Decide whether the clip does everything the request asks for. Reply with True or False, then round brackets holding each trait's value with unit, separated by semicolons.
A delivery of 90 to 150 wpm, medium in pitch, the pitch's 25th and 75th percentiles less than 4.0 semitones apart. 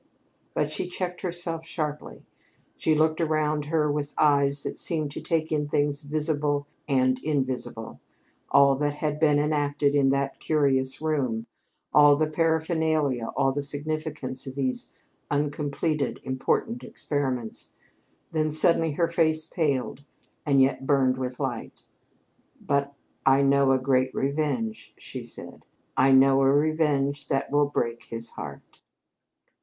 True (135 wpm; 145 Hz; 2.4 semitones)